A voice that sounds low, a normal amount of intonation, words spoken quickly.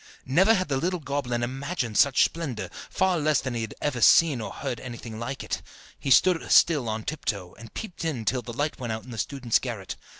Yes: low, 130 Hz; average, 4.8 semitones; fast, 210 wpm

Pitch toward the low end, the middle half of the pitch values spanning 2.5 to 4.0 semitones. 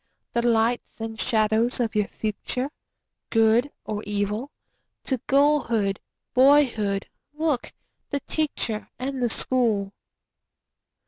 No: high, 235 Hz; average, 3.6 semitones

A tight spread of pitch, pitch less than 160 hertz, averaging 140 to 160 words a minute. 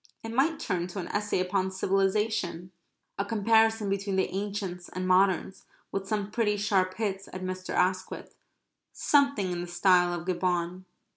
No: narrow, 2.2 semitones; high, 190 Hz; average, 155 wpm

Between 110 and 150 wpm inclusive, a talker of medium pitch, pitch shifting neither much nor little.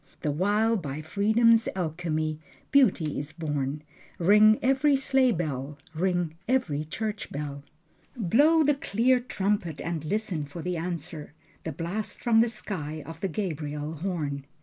No: average, 140 wpm; medium, 175 Hz; wide, 6.1 semitones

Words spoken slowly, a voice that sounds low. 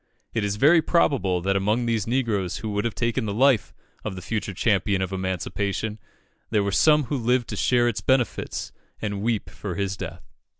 No: average, 190 wpm; low, 105 Hz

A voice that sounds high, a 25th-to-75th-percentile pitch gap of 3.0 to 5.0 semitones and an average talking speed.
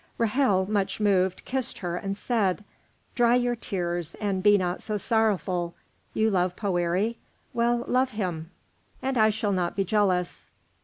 Yes: high, 205 Hz; average, 3.8 semitones; average, 150 wpm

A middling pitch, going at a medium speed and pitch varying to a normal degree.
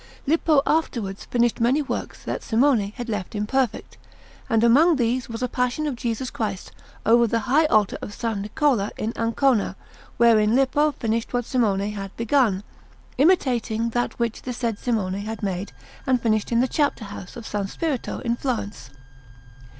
No: high, 235 Hz; average, 165 wpm; average, 3.5 semitones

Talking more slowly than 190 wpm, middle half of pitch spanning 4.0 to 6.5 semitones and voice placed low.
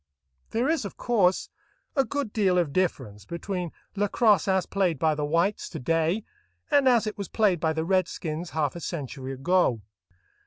No: average, 170 wpm; average, 4.7 semitones; medium, 180 Hz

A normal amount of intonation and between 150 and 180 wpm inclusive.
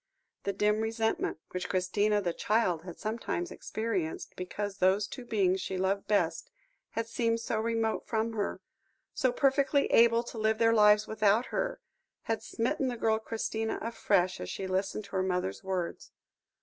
Yes: average, 3.2 semitones; average, 160 wpm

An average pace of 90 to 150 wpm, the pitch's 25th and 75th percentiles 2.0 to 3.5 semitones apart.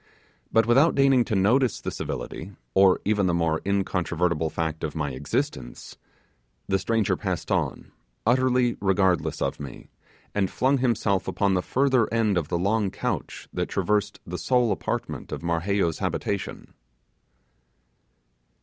No: average, 140 wpm; average, 5.1 semitones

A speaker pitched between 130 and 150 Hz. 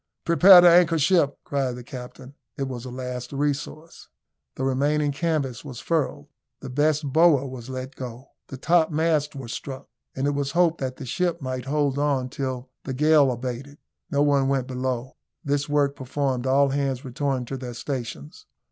Yes: low, 135 Hz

